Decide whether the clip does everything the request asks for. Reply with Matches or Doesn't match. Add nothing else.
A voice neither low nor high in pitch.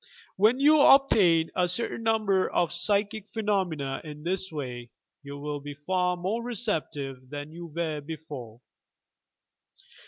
Matches